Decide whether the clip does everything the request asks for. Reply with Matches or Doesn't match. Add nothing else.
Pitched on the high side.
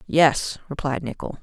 Doesn't match